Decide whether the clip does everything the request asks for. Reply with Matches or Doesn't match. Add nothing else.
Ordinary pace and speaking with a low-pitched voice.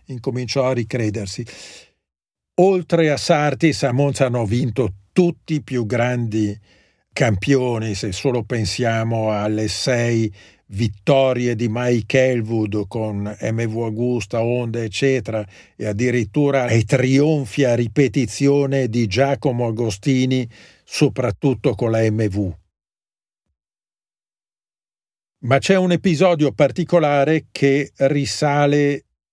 Doesn't match